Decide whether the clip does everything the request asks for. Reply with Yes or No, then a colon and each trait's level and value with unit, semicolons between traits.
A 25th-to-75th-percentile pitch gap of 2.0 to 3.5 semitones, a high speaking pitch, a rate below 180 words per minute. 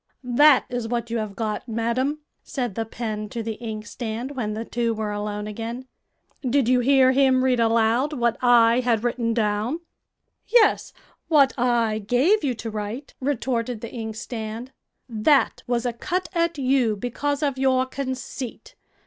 Yes: average, 2.8 semitones; high, 240 Hz; average, 155 wpm